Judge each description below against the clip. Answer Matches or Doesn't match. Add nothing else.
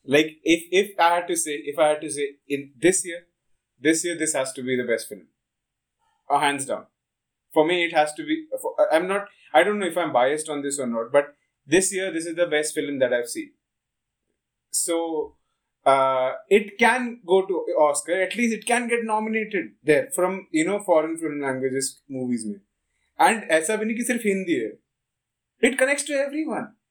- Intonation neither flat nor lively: Doesn't match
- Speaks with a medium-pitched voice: Matches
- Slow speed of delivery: Doesn't match